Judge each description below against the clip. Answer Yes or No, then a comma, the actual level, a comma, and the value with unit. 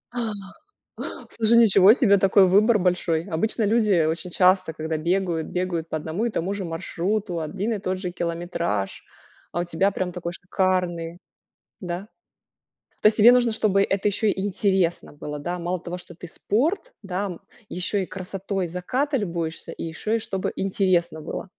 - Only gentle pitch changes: No, average, 3.0 semitones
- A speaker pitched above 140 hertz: Yes, medium, 185 Hz